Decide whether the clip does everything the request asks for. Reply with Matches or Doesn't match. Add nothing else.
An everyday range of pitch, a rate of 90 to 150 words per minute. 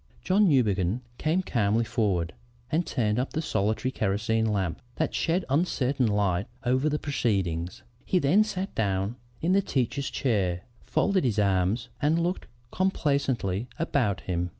Doesn't match